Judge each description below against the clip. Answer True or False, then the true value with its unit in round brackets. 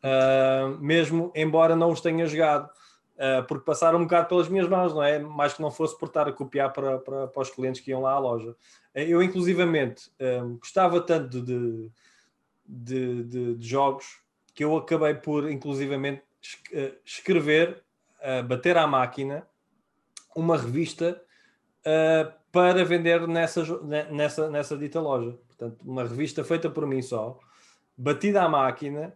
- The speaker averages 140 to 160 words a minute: True (155 wpm)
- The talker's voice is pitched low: False (150 Hz)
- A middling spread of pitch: True (3.8 semitones)